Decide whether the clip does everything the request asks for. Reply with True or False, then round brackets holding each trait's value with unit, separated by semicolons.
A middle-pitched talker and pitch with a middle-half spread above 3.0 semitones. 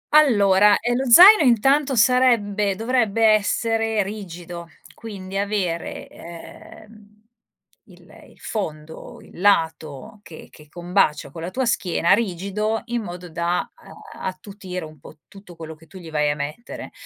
False (200 Hz; 4.7 semitones)